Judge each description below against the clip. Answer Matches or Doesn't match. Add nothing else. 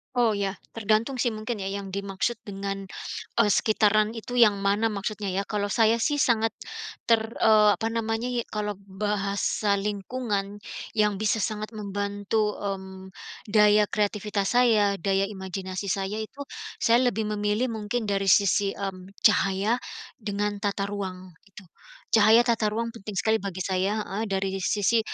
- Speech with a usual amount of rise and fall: Doesn't match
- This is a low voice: Doesn't match